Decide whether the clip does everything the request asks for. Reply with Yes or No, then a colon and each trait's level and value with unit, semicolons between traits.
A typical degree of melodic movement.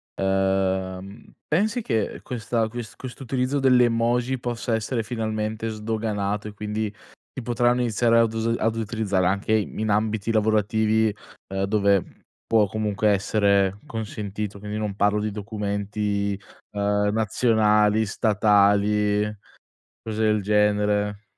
No: narrow, 1.7 semitones